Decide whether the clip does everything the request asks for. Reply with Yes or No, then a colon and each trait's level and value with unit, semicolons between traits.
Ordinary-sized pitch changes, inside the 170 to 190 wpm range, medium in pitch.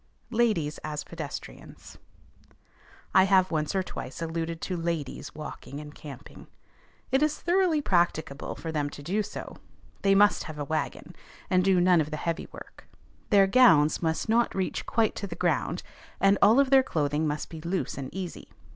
Yes: average, 4.6 semitones; average, 175 wpm; medium, 170 Hz